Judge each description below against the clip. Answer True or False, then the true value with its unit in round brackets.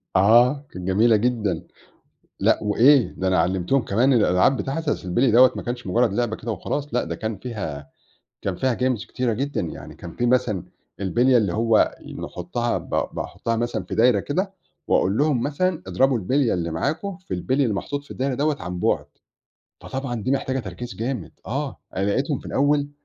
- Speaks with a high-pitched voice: False (120 Hz)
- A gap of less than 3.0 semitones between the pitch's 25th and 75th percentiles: False (5.4 semitones)